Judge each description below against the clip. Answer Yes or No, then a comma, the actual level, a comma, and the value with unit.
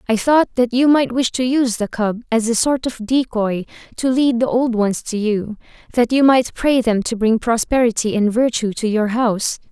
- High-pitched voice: Yes, high, 235 Hz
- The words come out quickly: Yes, fast, 215 wpm